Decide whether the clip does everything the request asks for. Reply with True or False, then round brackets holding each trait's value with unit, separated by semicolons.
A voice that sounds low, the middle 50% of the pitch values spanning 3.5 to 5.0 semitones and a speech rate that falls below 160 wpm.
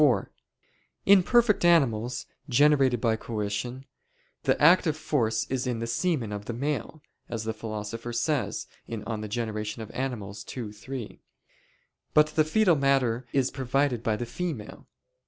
True (120 Hz; 4.7 semitones; 135 wpm)